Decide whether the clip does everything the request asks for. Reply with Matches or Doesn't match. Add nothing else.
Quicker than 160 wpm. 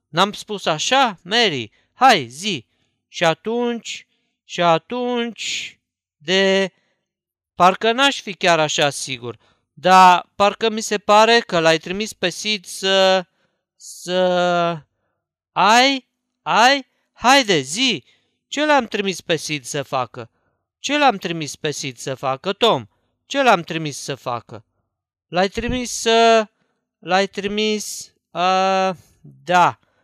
Doesn't match